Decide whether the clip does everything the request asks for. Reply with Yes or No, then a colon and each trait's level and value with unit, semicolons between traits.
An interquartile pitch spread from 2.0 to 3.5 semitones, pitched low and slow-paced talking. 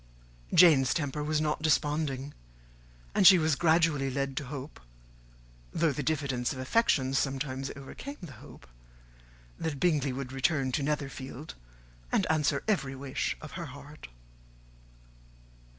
No: average, 2.7 semitones; medium, 145 Hz; slow, 130 wpm